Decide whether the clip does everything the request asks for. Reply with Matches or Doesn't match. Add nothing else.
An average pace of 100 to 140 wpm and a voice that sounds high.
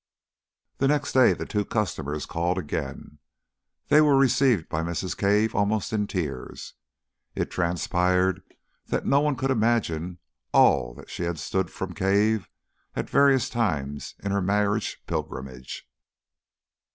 Doesn't match